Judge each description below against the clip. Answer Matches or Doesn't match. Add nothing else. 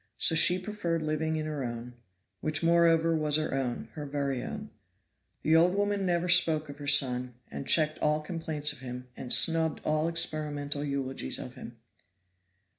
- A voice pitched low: Doesn't match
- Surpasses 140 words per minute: Matches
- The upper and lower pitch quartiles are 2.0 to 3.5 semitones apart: Matches